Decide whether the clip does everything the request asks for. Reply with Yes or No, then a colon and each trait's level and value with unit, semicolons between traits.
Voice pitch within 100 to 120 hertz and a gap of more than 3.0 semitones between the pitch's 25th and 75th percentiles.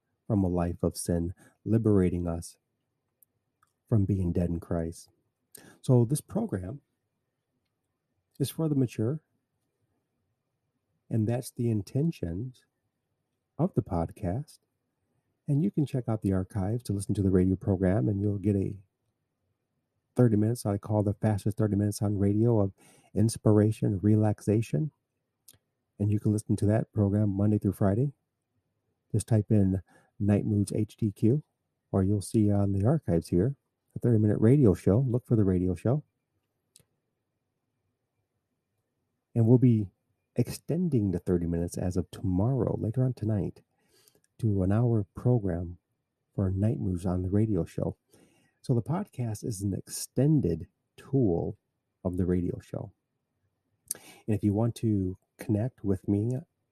Yes: low, 110 Hz; average, 3.9 semitones